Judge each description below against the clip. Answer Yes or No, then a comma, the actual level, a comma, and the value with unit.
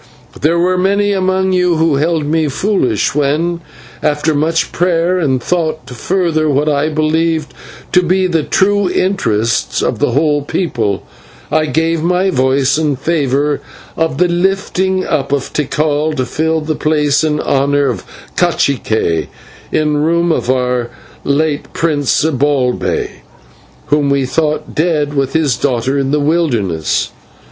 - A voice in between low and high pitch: Yes, medium, 155 Hz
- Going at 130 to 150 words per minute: Yes, average, 145 wpm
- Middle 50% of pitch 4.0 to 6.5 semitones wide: No, average, 3.3 semitones